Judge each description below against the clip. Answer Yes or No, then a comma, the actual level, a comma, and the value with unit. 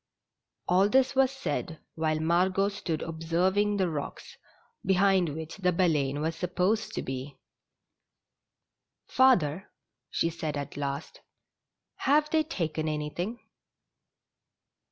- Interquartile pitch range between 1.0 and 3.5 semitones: No, average, 4.4 semitones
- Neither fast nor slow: No, slow, 115 wpm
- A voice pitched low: No, medium, 175 Hz